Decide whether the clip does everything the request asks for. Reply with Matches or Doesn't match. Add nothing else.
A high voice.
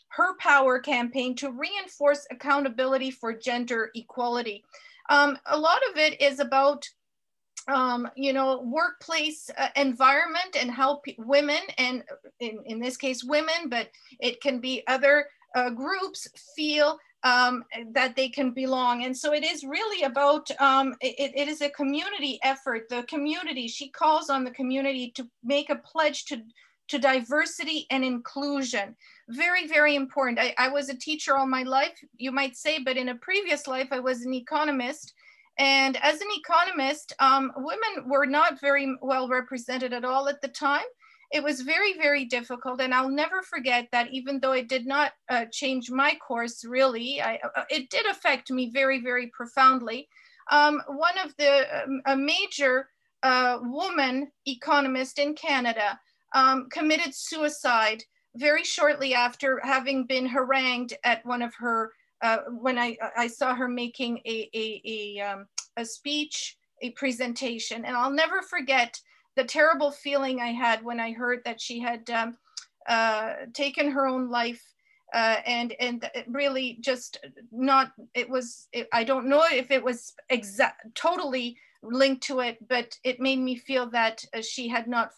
Matches